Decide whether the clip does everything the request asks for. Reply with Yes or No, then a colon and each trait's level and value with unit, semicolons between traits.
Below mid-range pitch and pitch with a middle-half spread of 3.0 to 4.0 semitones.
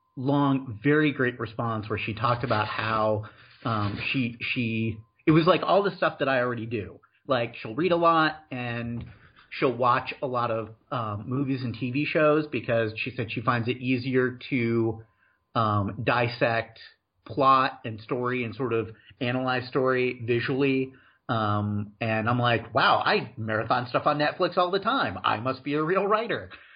Yes: low, 125 Hz; average, 3.5 semitones